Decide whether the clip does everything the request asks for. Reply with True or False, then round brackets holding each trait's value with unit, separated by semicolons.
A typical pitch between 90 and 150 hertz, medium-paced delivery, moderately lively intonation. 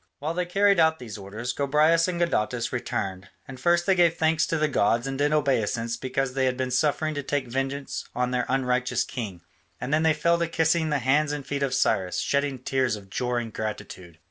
False (135 Hz; 215 wpm; 4.1 semitones)